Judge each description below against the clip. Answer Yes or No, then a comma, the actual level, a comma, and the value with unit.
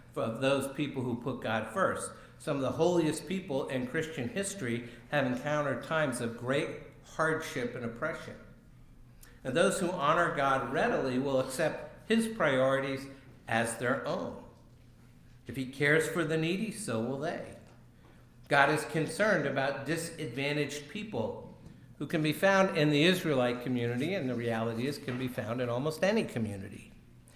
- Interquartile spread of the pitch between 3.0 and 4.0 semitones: No, average, 4.5 semitones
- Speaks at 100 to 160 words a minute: Yes, average, 155 wpm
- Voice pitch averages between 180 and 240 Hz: No, low, 135 Hz